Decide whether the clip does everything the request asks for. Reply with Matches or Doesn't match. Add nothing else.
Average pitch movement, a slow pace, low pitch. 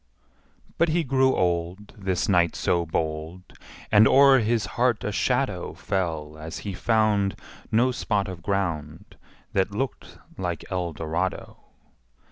Matches